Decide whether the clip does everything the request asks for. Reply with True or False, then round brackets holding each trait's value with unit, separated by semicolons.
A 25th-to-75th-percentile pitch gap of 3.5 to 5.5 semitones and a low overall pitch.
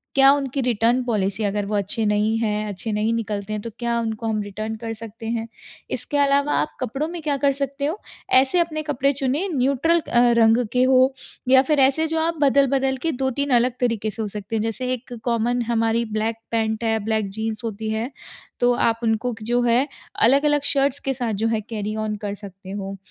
False (3.9 semitones; 235 Hz)